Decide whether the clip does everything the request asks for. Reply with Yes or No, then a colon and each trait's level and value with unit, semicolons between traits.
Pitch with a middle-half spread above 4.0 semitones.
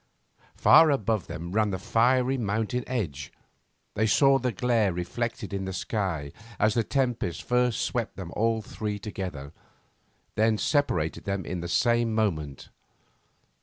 Yes: average, 4.4 semitones